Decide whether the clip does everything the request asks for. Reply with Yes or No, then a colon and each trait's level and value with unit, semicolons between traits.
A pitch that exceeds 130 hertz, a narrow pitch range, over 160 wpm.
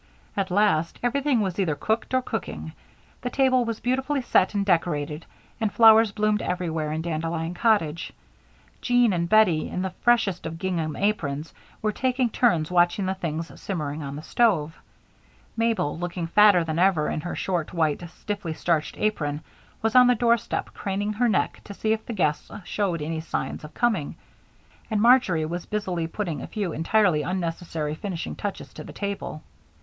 No: medium, 185 Hz; average, 5.1 semitones; average, 170 wpm